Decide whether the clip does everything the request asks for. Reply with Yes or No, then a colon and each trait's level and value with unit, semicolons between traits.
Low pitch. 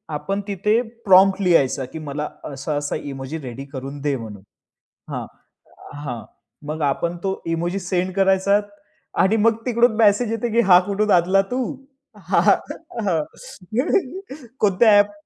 No: high, 190 Hz